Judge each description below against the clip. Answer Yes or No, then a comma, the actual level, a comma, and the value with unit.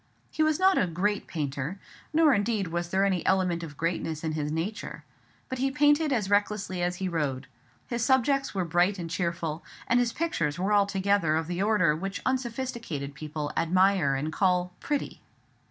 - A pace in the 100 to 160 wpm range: No, average, 175 wpm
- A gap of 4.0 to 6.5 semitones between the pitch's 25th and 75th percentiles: Yes, wide, 5.5 semitones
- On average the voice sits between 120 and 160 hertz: No, medium, 185 Hz